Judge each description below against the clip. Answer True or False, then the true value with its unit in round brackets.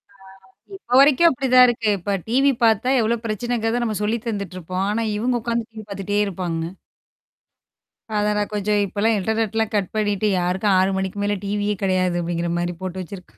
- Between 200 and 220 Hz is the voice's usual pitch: True (210 Hz)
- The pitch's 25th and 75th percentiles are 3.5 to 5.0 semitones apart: False (3.1 semitones)